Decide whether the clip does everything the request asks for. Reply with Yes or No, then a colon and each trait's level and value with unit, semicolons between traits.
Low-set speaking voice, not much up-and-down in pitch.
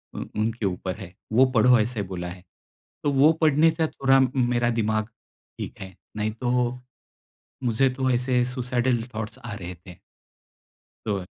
No: low, 120 Hz; average, 3.3 semitones